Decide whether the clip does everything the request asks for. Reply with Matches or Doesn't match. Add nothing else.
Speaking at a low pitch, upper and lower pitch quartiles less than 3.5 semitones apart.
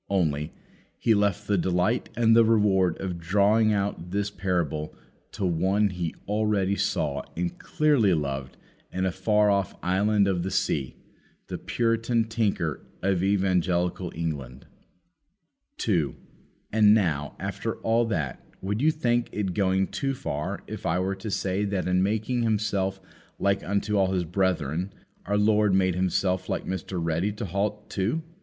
Matches